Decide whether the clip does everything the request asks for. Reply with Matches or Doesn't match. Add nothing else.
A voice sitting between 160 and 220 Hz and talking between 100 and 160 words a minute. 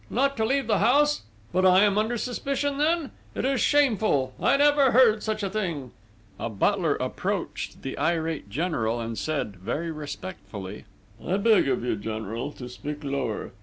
Doesn't match